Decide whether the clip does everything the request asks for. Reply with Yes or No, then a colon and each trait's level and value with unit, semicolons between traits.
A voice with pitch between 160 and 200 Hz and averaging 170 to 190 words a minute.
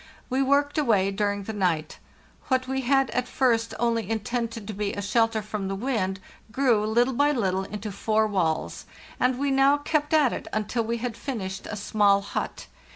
No: high, 225 Hz; average, 185 wpm